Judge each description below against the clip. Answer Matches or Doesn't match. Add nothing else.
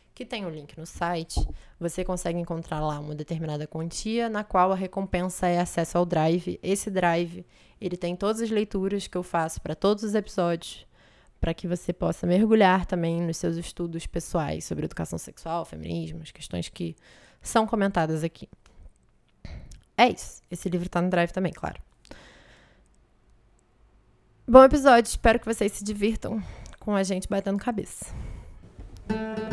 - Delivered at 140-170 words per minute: Matches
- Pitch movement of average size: Matches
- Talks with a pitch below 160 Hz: Doesn't match